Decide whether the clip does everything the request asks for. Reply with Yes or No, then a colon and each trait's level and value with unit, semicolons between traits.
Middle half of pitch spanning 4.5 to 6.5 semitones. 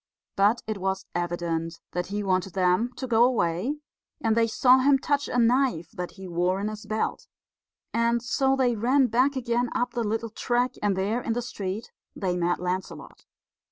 Yes: average, 4.8 semitones